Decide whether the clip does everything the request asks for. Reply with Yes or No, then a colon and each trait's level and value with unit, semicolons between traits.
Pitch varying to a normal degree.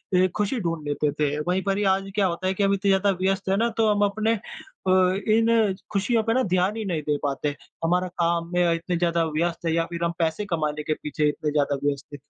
Yes: average, 3.6 semitones